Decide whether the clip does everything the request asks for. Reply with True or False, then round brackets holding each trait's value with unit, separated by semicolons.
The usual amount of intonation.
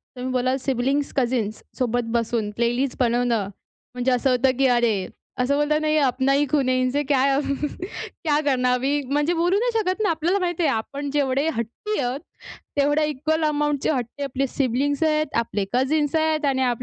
True (3.3 semitones)